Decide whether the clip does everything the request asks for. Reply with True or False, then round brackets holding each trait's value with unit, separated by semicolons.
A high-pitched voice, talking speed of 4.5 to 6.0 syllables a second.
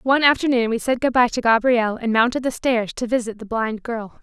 True (240 Hz; 5.5 syllables/s)